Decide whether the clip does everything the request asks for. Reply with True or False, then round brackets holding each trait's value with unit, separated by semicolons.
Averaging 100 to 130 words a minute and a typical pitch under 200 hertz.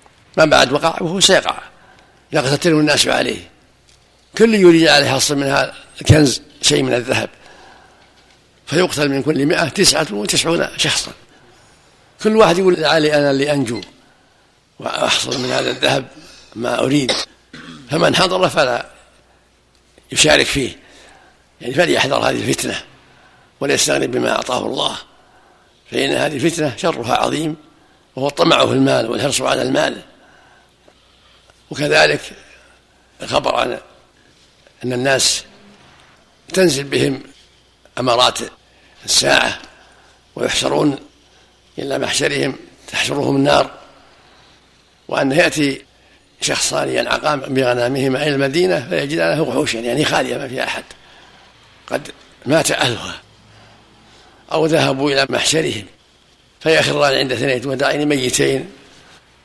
True (105 wpm; 135 Hz)